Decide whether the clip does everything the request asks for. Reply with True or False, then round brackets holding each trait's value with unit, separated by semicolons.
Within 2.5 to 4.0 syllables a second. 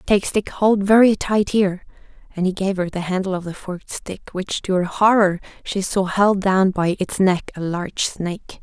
False (4.8 syllables/s)